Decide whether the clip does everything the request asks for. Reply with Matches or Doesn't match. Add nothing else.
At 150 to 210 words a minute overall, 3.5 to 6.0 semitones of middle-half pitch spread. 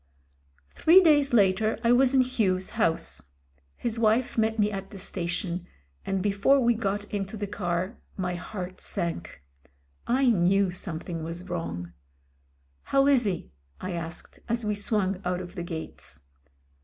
Matches